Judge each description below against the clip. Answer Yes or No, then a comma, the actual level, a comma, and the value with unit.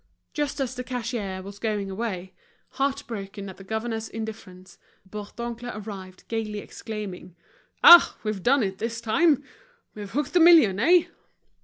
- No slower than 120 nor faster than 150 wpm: Yes, average, 145 wpm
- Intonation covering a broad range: No, average, 3.7 semitones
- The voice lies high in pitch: Yes, high, 220 Hz